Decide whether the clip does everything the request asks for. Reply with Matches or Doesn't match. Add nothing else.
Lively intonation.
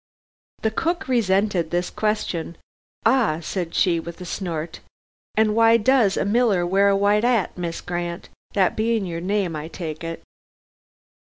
Doesn't match